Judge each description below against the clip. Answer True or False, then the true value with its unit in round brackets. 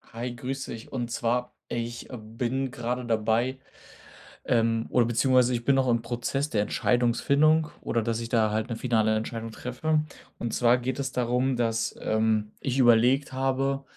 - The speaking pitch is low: True (120 Hz)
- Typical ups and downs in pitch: False (2.2 semitones)